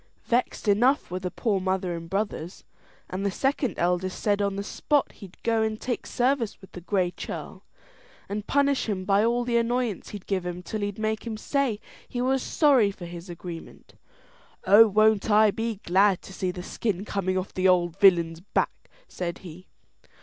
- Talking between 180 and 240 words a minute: Yes, average, 185 wpm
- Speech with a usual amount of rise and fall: Yes, average, 3.6 semitones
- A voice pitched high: Yes, high, 200 Hz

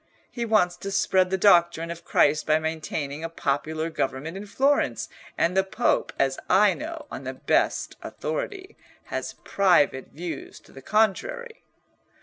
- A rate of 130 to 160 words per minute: Yes, average, 150 wpm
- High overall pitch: No, medium, 180 Hz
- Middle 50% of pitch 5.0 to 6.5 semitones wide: Yes, average, 5.3 semitones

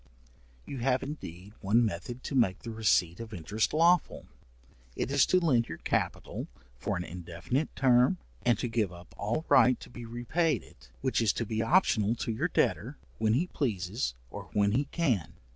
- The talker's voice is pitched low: Yes, low, 115 Hz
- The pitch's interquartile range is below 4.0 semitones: No, average, 4.7 semitones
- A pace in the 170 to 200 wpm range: Yes, average, 180 wpm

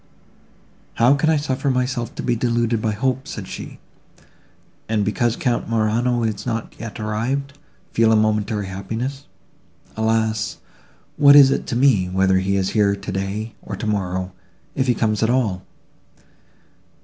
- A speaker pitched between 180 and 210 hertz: No, low, 110 Hz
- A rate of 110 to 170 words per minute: Yes, average, 150 wpm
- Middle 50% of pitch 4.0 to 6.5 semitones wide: No, average, 3.3 semitones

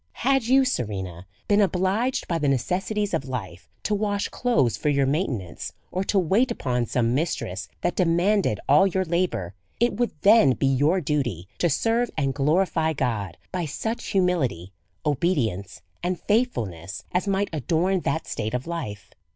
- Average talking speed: Yes, average, 160 wpm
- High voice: No, medium, 160 Hz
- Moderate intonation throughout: No, wide, 7.8 semitones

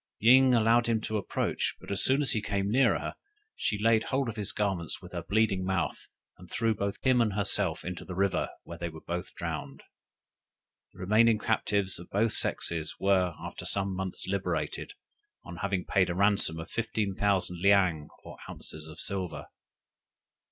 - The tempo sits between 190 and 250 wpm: No, average, 175 wpm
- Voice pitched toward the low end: Yes, low, 100 Hz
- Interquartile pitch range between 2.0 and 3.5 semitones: Yes, average, 3.2 semitones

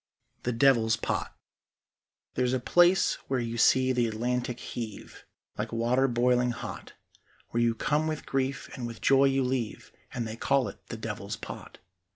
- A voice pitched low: Yes, low, 125 Hz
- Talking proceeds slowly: No, average, 165 wpm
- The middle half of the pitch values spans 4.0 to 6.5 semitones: No, narrow, 2.4 semitones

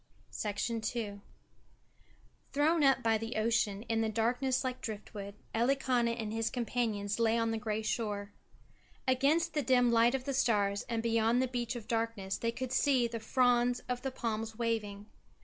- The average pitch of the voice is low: No, high, 230 Hz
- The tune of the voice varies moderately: No, narrow, 2.3 semitones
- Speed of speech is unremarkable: Yes, average, 165 wpm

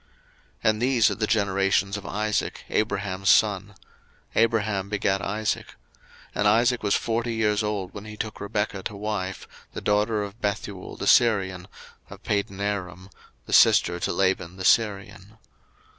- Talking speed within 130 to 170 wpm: Yes, average, 150 wpm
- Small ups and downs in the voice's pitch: Yes, narrow, 1.7 semitones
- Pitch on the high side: No, low, 105 Hz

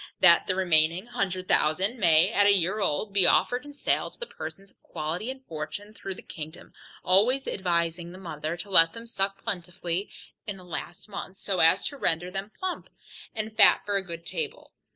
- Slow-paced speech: No, average, 195 wpm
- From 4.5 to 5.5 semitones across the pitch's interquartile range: No, average, 3.7 semitones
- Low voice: No, high, 190 Hz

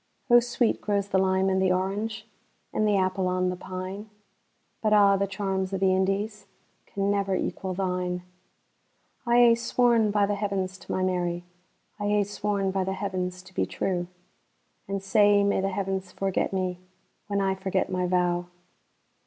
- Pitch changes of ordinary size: No, narrow, 1.8 semitones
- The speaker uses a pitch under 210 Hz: Yes, high, 190 Hz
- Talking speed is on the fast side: No, average, 150 wpm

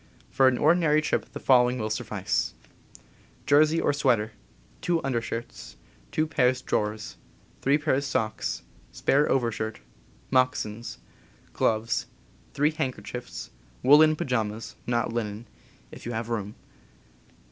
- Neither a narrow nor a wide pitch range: Yes, average, 4.3 semitones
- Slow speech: Yes, slow, 115 wpm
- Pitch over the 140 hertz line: No, low, 125 Hz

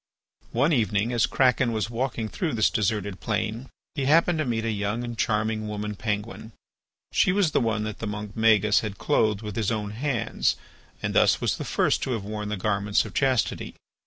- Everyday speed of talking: Yes, average, 195 wpm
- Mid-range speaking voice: No, low, 110 Hz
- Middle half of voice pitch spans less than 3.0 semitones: Yes, narrow, 2.4 semitones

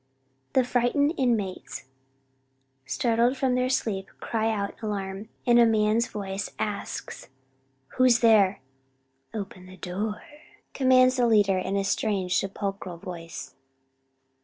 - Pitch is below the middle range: No, high, 210 Hz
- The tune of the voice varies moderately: Yes, average, 3.7 semitones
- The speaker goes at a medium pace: No, slow, 120 wpm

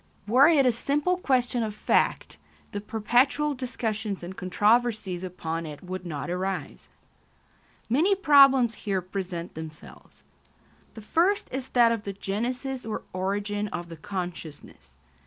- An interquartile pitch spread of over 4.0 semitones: Yes, wide, 5.6 semitones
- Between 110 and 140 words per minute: Yes, slow, 135 wpm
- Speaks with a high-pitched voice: Yes, high, 210 Hz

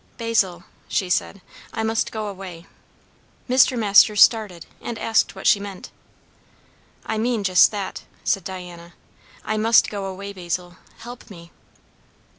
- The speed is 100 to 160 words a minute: Yes, slow, 135 wpm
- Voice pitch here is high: Yes, high, 200 Hz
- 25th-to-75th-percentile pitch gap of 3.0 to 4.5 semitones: Yes, average, 3.4 semitones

